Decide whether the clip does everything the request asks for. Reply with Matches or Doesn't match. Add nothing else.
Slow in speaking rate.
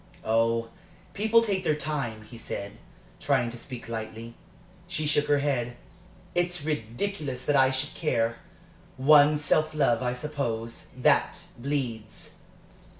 Matches